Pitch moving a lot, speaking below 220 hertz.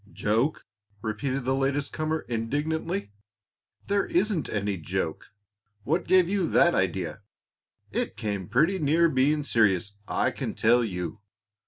Yes: wide, 6.9 semitones; low, 135 Hz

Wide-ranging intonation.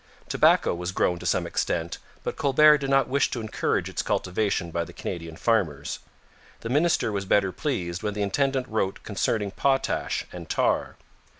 Yes: wide, 7.2 semitones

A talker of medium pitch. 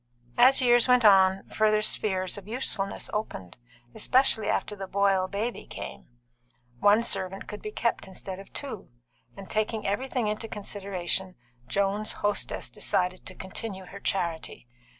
No: high, 200 Hz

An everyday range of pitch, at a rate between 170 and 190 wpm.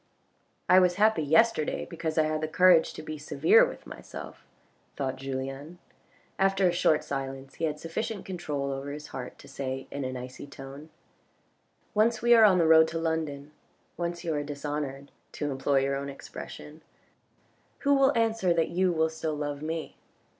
Yes: average, 4.0 semitones; average, 175 wpm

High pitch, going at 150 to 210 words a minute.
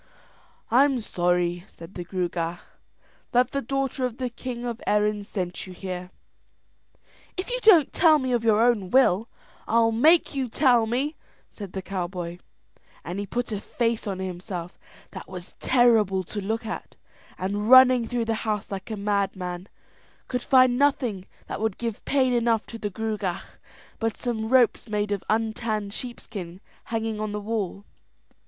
Yes: high, 220 Hz; average, 160 wpm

